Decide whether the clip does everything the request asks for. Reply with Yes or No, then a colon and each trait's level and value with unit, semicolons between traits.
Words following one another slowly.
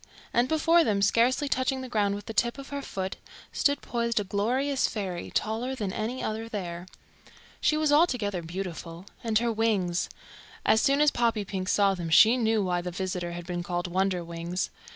No: average, 180 wpm